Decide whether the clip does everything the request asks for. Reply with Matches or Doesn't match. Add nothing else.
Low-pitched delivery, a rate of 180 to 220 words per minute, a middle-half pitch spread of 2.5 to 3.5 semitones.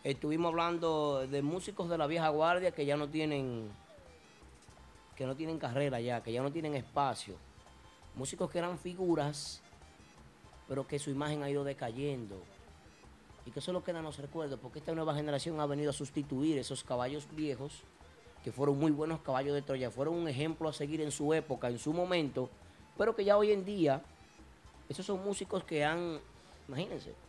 Doesn't match